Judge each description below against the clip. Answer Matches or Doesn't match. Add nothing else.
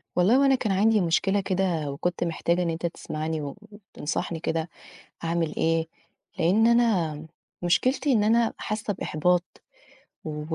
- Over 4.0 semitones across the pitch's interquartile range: Matches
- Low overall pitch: Doesn't match